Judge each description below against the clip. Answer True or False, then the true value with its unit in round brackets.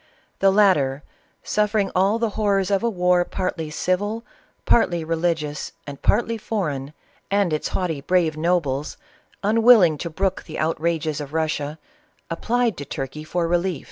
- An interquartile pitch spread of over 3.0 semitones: True (4.5 semitones)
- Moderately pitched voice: True (175 Hz)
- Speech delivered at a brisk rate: False (155 wpm)